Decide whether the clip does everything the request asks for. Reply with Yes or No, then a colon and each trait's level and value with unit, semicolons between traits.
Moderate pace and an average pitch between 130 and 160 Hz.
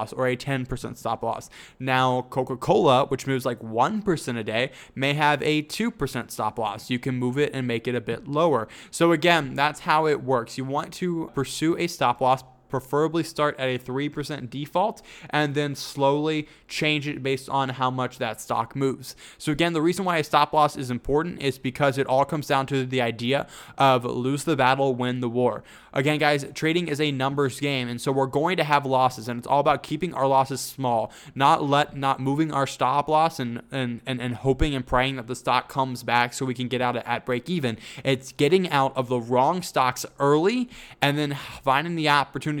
No: fast, 210 wpm; low, 135 Hz